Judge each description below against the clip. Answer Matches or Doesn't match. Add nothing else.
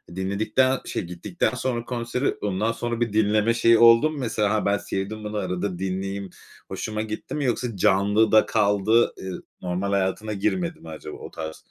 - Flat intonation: Doesn't match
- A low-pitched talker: Matches